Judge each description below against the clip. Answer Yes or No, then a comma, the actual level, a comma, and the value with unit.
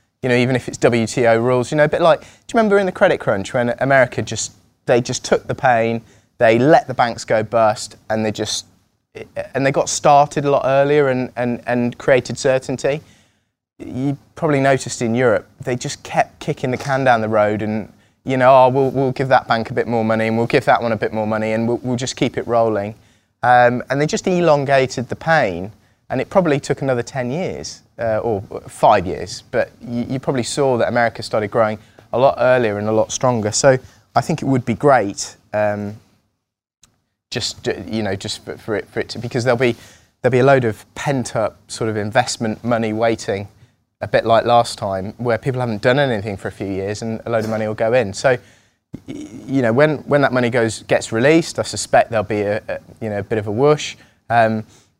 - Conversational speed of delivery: No, fast, 220 wpm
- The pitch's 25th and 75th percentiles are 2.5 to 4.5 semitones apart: Yes, average, 3.2 semitones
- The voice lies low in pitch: Yes, low, 120 Hz